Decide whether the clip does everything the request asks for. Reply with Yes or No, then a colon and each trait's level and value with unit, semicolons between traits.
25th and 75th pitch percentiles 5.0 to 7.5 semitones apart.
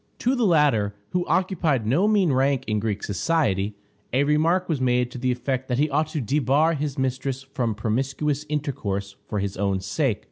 Yes: wide, 5.5 semitones